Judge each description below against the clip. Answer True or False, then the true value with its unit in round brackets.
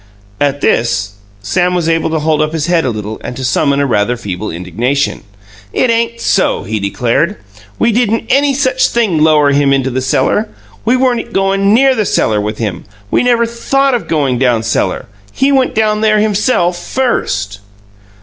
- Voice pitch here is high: False (160 Hz)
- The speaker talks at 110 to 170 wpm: False (180 wpm)